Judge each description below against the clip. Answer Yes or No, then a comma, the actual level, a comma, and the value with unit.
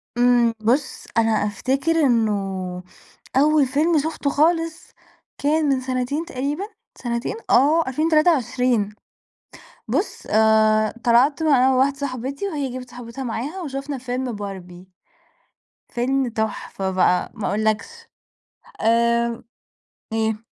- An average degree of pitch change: Yes, average, 4.6 semitones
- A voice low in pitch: No, very high, 250 Hz